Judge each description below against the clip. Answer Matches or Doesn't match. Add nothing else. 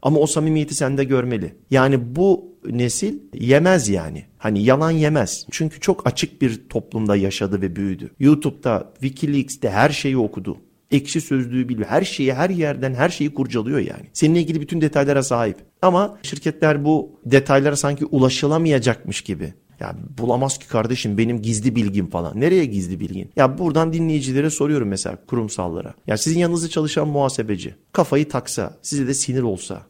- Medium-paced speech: Doesn't match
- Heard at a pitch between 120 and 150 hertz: Matches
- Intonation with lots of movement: Doesn't match